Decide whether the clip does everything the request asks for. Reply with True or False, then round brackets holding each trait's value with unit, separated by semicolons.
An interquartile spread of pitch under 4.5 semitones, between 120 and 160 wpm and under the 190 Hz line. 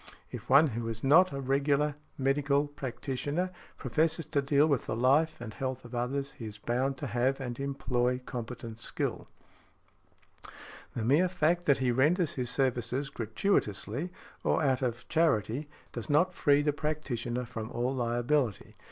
True (3.4 semitones; 155 wpm; 135 Hz)